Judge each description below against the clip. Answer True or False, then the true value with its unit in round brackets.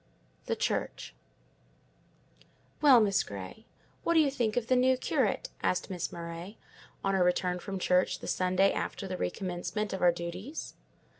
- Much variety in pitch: False (4.3 semitones)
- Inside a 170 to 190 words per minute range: False (155 wpm)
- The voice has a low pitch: False (190 Hz)